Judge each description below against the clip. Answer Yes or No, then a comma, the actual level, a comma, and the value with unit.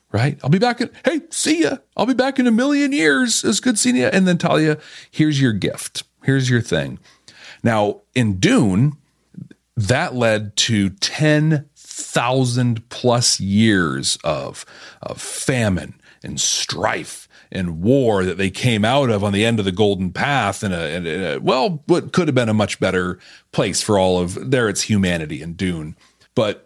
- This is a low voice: Yes, low, 125 Hz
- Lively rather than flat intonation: Yes, wide, 7.6 semitones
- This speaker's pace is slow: No, average, 175 wpm